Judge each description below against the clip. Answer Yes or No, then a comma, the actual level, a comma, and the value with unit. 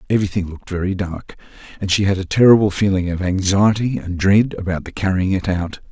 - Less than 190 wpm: No, average, 195 wpm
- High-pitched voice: No, very low, 95 Hz